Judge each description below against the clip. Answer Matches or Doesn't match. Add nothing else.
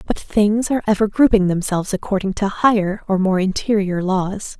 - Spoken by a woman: Matches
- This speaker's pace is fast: Doesn't match